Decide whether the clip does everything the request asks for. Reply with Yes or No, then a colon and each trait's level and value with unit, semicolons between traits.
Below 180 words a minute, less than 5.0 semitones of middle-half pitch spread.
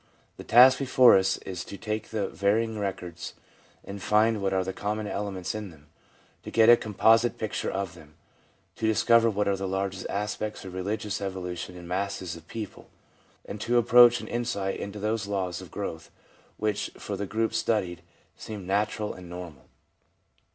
Yes: average, 170 wpm; average, 2.8 semitones